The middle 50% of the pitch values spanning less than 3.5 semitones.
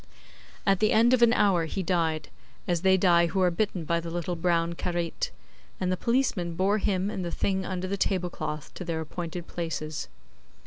Yes: narrow, 2.4 semitones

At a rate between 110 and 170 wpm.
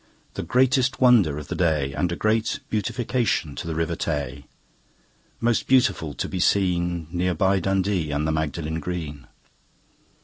Yes: average, 150 wpm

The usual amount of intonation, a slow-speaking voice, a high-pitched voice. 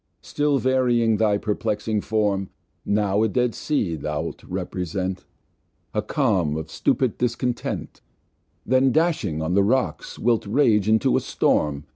No: average, 4.6 semitones; slow, 130 wpm; low, 105 Hz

